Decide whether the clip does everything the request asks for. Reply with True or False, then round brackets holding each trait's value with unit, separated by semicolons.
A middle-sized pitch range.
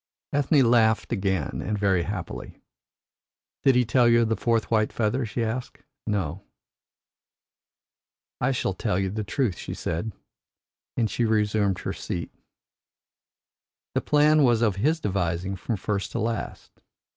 True (3.6 semitones)